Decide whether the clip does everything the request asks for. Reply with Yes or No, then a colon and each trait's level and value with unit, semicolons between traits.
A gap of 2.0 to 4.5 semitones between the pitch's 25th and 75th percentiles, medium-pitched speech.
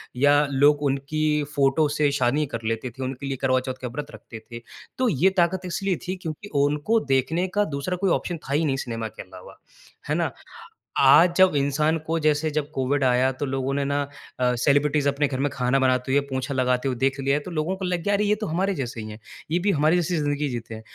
Yes: average, 3.5 semitones; medium, 145 Hz